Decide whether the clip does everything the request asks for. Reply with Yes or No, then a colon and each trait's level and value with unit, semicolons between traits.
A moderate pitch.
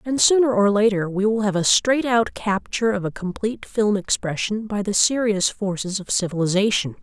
No: high, 210 Hz